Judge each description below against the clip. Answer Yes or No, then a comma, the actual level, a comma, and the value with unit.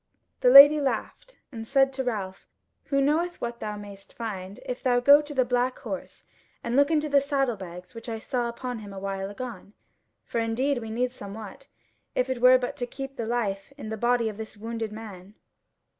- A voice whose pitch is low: No, high, 240 Hz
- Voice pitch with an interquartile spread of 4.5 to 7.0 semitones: No, average, 4.0 semitones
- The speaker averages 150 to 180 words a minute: No, average, 200 wpm